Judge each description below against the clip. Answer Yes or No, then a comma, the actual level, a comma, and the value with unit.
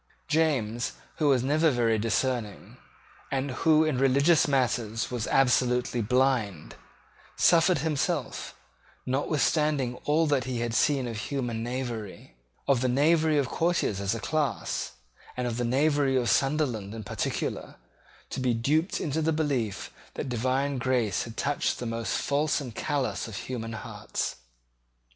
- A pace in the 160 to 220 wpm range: No, average, 145 wpm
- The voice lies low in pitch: Yes, low, 130 Hz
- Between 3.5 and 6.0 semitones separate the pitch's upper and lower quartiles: Yes, average, 3.9 semitones